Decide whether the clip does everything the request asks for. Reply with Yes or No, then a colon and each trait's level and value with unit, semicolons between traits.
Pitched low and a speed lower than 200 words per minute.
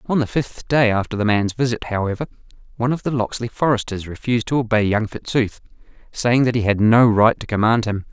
No: low, 115 Hz; fast, 205 wpm